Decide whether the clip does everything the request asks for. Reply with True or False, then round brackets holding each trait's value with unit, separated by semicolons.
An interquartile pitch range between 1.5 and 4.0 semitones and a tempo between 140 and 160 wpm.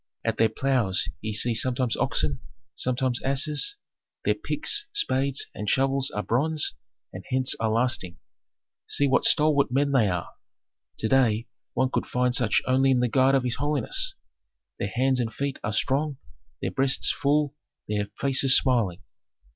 True (3.3 semitones; 155 wpm)